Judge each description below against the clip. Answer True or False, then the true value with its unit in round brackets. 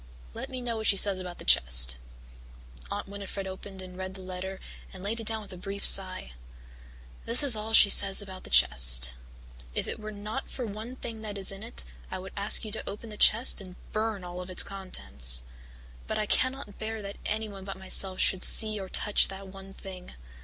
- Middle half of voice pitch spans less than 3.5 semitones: True (2.5 semitones)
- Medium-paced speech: False (210 wpm)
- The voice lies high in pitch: True (195 Hz)